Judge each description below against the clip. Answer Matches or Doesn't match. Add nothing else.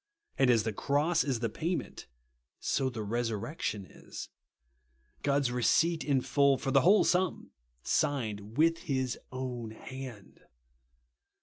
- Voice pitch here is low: Matches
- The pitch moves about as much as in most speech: Matches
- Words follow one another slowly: Matches